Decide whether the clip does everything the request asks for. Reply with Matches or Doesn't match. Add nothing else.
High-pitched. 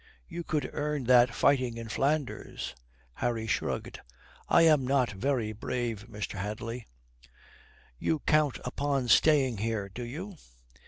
Doesn't match